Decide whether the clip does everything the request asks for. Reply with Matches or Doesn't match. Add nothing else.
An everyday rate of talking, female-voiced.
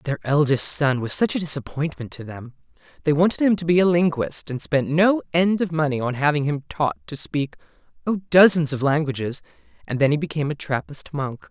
Doesn't match